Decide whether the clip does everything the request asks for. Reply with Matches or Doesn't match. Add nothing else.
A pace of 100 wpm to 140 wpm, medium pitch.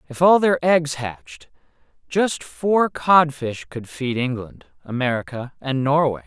Matches